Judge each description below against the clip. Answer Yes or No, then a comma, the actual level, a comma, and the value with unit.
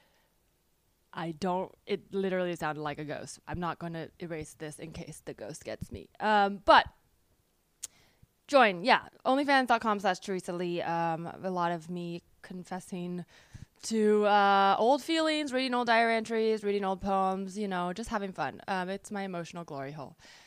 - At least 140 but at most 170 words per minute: Yes, average, 165 wpm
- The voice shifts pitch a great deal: No, average, 3.6 semitones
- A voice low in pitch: No, medium, 185 Hz